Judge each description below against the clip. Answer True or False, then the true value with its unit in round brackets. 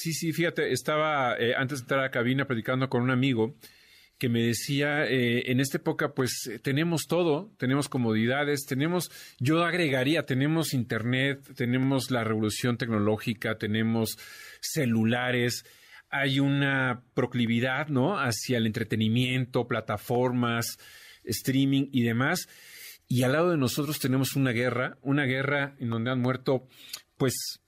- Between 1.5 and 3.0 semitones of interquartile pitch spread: True (2.7 semitones)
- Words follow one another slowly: False (140 wpm)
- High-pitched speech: False (130 Hz)